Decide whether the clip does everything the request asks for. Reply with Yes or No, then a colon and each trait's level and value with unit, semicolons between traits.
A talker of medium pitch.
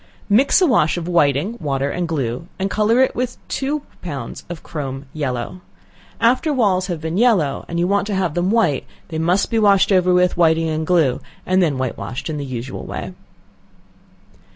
Yes: medium, 175 Hz